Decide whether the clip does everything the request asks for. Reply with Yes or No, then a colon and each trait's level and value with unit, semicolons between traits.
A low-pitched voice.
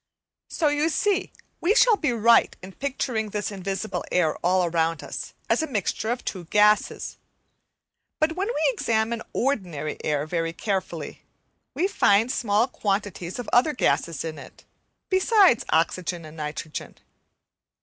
No: high, 210 Hz